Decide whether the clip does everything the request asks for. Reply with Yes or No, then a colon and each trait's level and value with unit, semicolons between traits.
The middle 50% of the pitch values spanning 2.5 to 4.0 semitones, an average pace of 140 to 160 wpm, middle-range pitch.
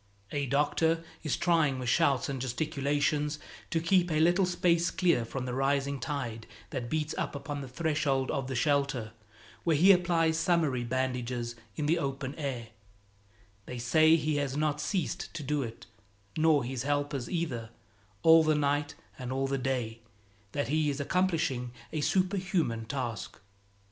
Yes: average, 3.7 semitones; average, 155 wpm; medium, 145 Hz